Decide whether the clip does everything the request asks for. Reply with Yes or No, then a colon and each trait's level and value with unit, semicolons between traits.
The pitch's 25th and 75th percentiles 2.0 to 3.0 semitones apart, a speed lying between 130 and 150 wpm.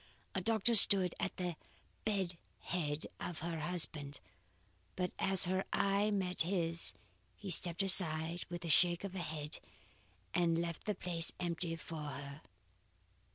Yes: narrow, 2.5 semitones; average, 145 wpm